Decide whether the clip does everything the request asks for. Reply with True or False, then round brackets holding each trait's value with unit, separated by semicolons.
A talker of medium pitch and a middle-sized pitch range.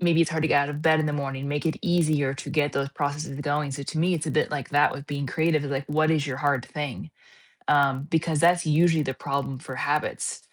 False (145 Hz; 2.1 semitones)